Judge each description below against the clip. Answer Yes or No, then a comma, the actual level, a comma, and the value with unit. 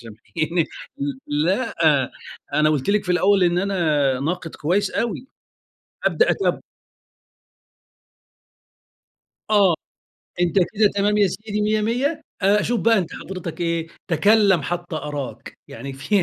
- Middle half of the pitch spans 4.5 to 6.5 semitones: Yes, average, 5.0 semitones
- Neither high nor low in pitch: Yes, medium, 180 Hz